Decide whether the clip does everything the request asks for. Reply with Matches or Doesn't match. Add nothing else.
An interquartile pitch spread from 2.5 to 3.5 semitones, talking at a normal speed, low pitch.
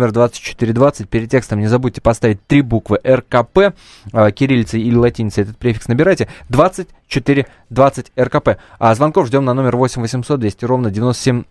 Matches